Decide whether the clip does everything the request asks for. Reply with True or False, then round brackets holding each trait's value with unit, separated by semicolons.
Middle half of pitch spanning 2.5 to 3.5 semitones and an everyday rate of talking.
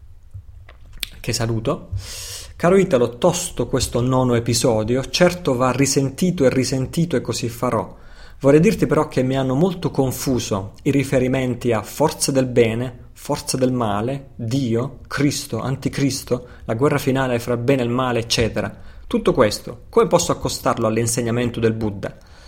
True (3.2 semitones; 145 wpm)